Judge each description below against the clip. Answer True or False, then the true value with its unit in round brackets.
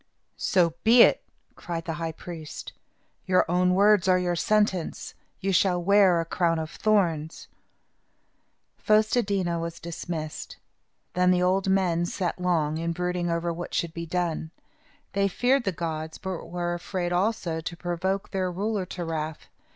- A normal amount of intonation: False (2.3 semitones)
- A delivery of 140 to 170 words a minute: True (160 wpm)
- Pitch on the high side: False (175 Hz)